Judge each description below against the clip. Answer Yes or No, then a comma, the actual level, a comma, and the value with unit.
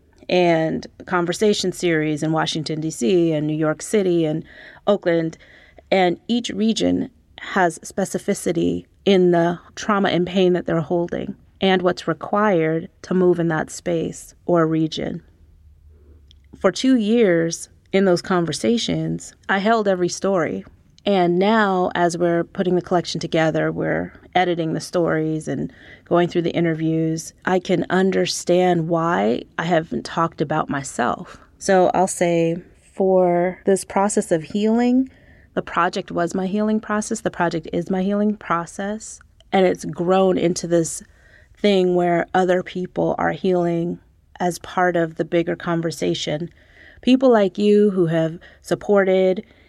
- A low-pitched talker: No, medium, 175 Hz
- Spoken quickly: No, average, 140 wpm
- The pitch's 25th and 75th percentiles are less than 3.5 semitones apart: Yes, average, 2.9 semitones